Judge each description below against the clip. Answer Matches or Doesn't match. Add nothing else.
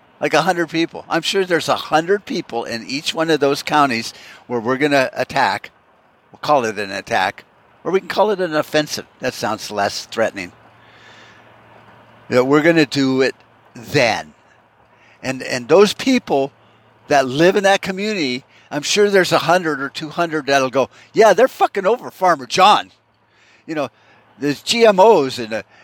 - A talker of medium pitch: Matches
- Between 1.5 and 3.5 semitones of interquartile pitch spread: Doesn't match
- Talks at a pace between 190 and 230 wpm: Doesn't match